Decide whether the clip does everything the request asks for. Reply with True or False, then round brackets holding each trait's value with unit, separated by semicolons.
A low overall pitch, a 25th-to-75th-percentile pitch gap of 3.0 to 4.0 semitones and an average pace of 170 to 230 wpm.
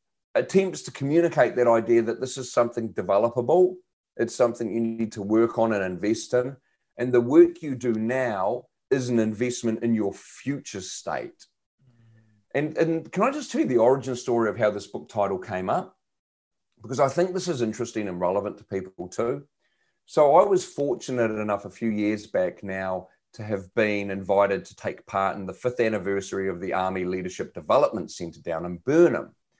False (115 Hz; 4.4 semitones; 185 wpm)